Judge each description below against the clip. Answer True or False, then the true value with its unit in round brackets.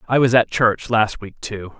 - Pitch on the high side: False (115 Hz)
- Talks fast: True (235 wpm)